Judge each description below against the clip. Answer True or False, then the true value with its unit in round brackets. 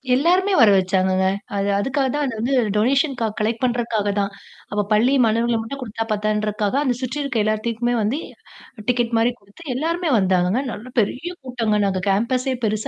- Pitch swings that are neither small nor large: True (3.7 semitones)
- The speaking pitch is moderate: False (230 Hz)